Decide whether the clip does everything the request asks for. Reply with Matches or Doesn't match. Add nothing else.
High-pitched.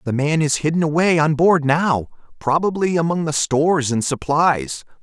Doesn't match